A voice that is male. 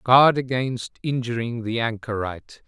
Yes: male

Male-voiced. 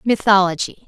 No: female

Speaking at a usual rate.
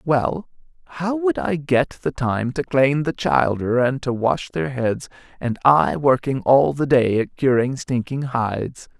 Yes: average, 165 wpm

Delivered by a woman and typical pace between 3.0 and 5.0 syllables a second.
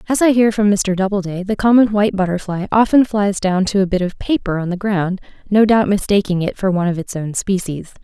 No: female; 5.8 syllables/s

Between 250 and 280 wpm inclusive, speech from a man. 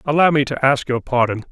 No: fast, 240 wpm; male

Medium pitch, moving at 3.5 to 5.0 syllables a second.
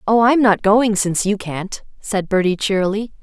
No: high, 205 Hz; 4.9 syllables/s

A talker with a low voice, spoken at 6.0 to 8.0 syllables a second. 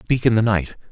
No: low, 105 Hz; 5.7 syllables/s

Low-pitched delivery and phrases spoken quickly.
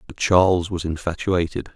No: very low, 90 Hz; slow, 135 wpm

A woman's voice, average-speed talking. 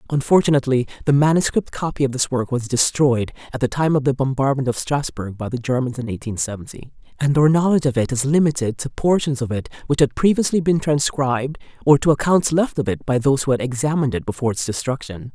No: female; fast, 210 wpm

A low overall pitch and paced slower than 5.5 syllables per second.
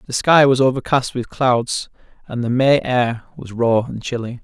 Yes: low, 125 Hz; 4.5 syllables/s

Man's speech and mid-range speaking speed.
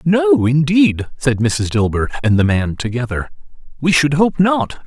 Yes: male; average, 160 wpm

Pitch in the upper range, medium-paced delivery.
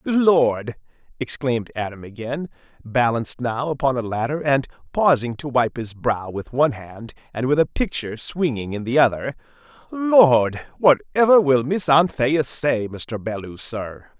No: low, 135 Hz; average, 150 wpm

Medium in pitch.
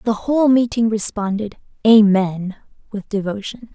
No: high, 215 Hz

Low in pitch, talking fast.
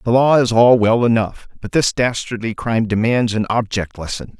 No: low, 115 Hz; average, 190 wpm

